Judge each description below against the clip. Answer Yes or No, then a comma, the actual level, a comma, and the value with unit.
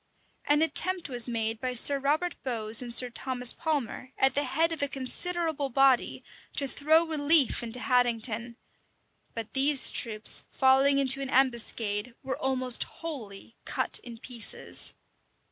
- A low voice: No, very high, 260 Hz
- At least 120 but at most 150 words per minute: Yes, average, 145 wpm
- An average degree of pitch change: Yes, average, 3.2 semitones